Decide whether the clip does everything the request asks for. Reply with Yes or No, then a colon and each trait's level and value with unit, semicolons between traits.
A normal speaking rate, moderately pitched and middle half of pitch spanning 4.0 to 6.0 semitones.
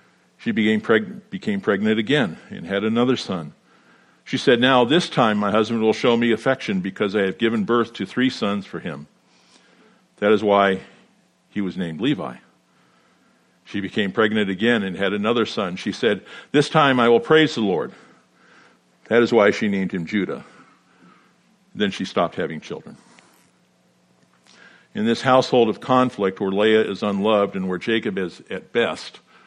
No: average, 165 wpm; low, 110 Hz; average, 4.5 semitones